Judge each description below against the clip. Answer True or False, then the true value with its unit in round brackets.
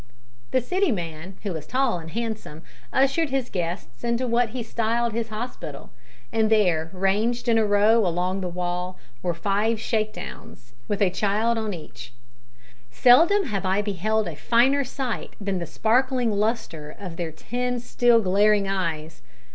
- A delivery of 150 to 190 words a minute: True (155 wpm)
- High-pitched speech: True (210 Hz)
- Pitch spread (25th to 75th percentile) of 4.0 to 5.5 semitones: True (4.8 semitones)